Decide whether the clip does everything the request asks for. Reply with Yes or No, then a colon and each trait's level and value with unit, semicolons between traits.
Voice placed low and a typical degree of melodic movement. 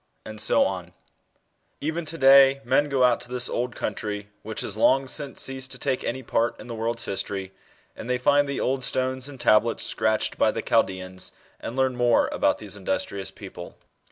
Yes: low, 125 Hz; average, 3.6 semitones